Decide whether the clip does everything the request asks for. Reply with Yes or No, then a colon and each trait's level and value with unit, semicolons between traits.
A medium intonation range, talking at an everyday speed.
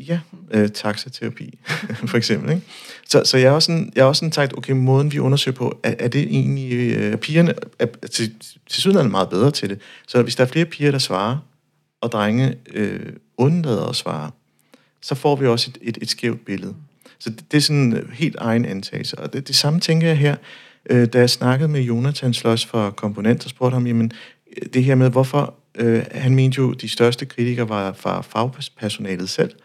Yes: average, 3.8 semitones; average, 210 wpm